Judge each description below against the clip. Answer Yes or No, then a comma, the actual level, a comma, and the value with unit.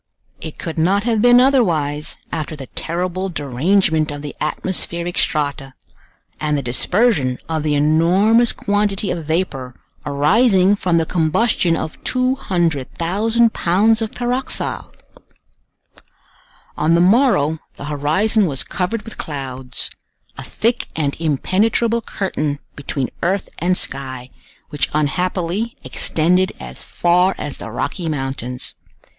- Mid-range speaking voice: Yes, medium, 170 Hz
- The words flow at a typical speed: No, slow, 120 wpm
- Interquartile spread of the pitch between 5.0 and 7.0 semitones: Yes, wide, 5.6 semitones